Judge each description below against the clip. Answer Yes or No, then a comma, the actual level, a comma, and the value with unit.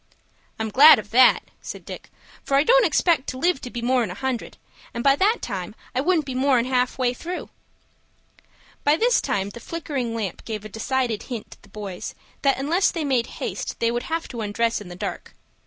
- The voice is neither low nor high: No, very high, 255 Hz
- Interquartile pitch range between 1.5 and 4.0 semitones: No, average, 4.6 semitones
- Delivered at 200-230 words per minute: Yes, fast, 205 wpm